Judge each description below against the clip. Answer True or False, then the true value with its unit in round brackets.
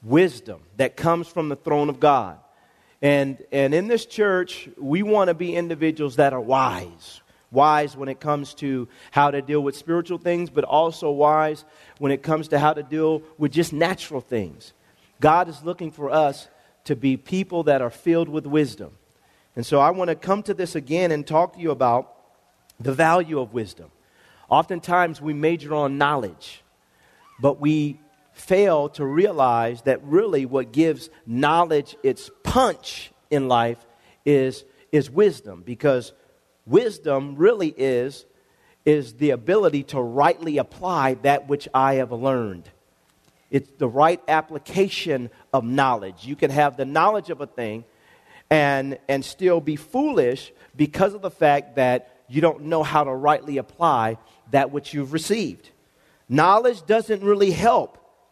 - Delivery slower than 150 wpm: False (155 wpm)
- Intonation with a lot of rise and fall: False (3.9 semitones)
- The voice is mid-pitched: True (150 Hz)